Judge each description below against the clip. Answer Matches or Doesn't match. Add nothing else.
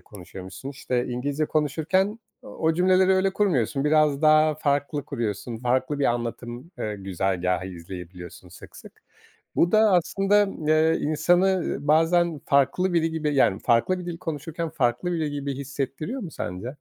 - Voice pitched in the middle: Matches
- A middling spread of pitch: Doesn't match